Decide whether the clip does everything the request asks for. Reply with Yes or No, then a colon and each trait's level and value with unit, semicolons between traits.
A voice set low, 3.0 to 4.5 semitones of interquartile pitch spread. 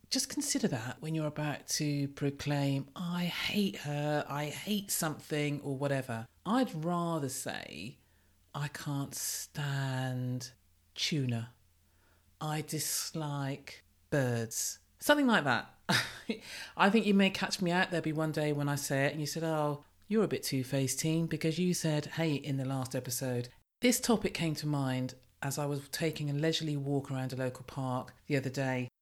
No: medium, 145 Hz; average, 3.6 semitones